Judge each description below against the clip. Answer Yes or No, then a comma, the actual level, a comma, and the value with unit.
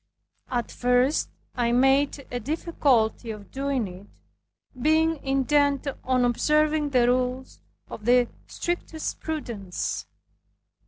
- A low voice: No, very high, 260 Hz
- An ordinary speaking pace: No, slow, 105 wpm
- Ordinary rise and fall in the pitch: Yes, average, 3.4 semitones